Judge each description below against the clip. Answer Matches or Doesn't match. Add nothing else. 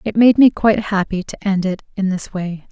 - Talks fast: Matches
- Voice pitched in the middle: Doesn't match